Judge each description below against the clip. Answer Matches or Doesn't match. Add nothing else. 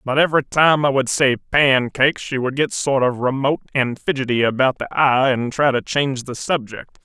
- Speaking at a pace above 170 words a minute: Matches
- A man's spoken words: Matches